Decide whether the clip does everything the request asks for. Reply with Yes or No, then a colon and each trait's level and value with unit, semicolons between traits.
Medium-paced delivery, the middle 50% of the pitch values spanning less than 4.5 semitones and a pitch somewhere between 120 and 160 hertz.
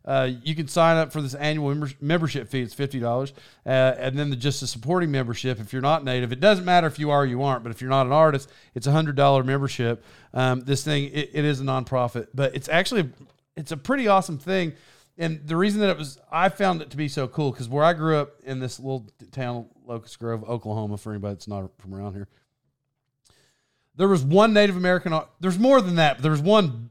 No: fast, 235 wpm; average, 3.8 semitones; medium, 140 Hz